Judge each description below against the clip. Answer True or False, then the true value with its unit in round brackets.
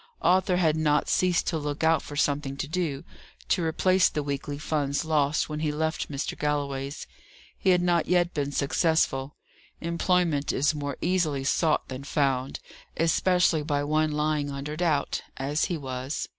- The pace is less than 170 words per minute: True (160 wpm)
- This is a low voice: False (150 Hz)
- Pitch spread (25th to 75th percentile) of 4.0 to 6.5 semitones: False (2.6 semitones)